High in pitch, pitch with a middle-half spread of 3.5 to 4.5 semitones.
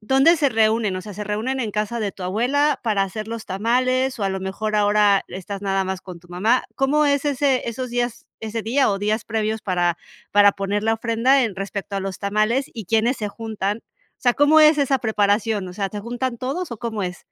Yes: high, 220 Hz; average, 4.0 semitones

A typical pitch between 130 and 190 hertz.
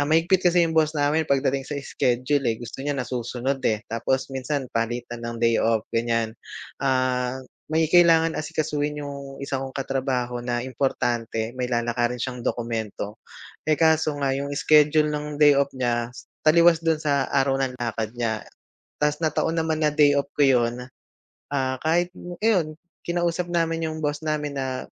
Yes: medium, 140 Hz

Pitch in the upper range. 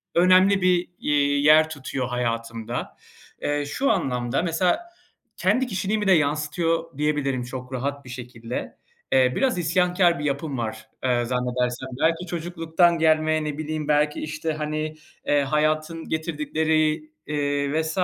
No: medium, 155 Hz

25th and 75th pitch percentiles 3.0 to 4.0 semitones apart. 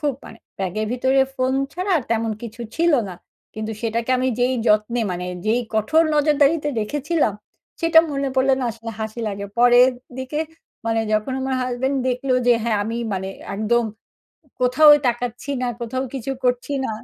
Yes: average, 3.4 semitones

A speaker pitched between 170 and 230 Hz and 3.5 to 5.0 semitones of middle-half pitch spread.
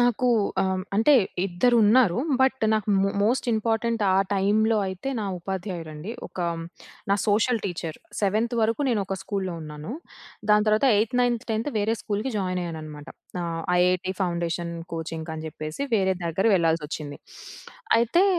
Yes: high, 195 Hz; average, 4.7 semitones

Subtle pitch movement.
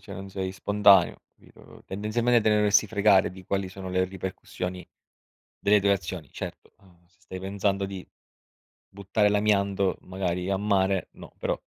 Yes: narrow, 1.6 semitones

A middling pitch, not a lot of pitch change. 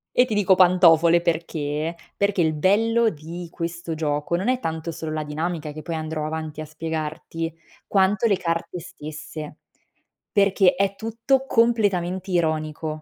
No: medium, 170 Hz; average, 3.6 semitones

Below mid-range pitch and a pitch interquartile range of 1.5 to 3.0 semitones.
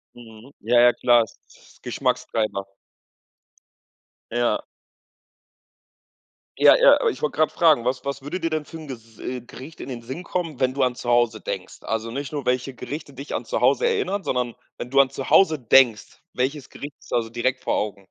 No: low, 130 Hz; average, 3.9 semitones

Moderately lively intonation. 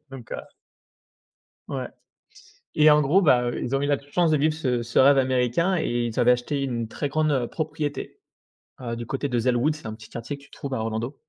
Yes: average, 3.8 semitones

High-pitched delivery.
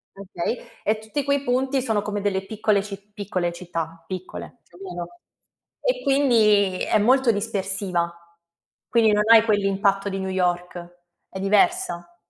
Yes: high, 200 Hz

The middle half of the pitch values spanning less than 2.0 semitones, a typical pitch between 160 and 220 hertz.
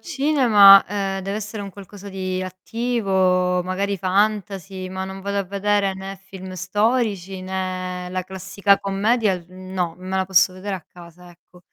Yes: narrow, 1.4 semitones; high, 190 Hz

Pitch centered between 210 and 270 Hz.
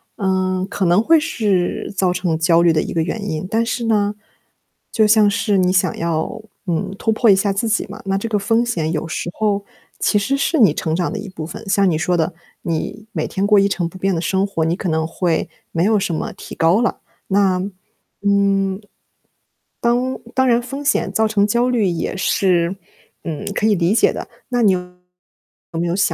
No: high, 195 Hz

